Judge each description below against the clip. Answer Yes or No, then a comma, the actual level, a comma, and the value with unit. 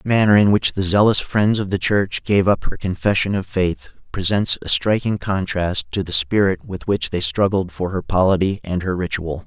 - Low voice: Yes, very low, 95 Hz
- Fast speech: Yes, fast, 215 wpm